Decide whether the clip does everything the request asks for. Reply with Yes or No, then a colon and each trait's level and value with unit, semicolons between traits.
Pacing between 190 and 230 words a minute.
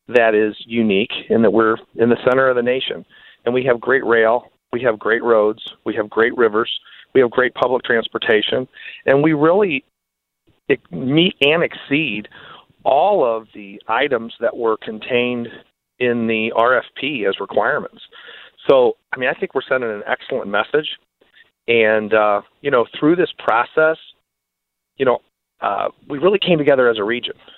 No: average, 165 wpm